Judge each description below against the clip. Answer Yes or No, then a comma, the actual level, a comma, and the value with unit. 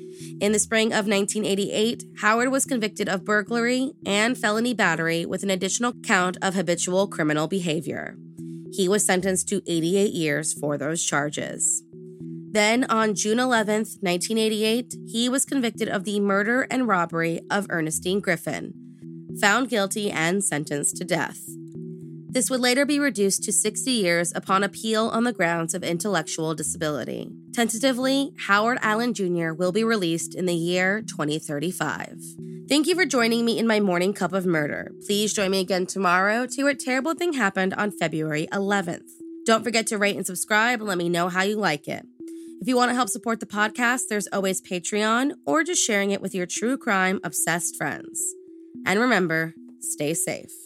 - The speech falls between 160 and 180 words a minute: Yes, average, 170 wpm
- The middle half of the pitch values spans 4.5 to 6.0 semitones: Yes, average, 4.9 semitones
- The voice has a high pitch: Yes, high, 200 Hz